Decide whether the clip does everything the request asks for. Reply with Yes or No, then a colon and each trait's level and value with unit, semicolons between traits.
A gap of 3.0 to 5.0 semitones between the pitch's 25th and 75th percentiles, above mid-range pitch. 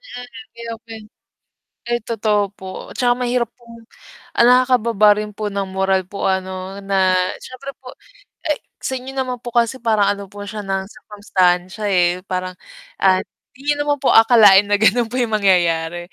Yes: average, 4.0 semitones; high, 210 Hz